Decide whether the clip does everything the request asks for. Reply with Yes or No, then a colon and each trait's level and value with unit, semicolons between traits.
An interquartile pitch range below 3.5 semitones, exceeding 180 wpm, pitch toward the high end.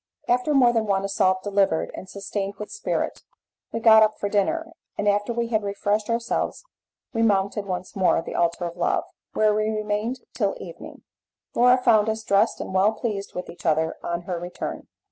Yes: average, 2.8 semitones; average, 190 wpm; high, 210 Hz